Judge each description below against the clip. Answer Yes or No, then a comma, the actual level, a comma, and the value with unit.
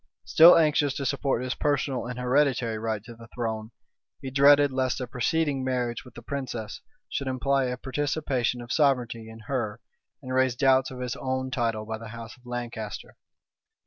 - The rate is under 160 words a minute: No, average, 175 wpm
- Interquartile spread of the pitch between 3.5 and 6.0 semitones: No, narrow, 2.6 semitones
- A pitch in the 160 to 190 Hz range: No, low, 125 Hz